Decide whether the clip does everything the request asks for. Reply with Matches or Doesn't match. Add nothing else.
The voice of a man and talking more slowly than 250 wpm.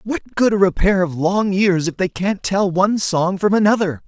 Matches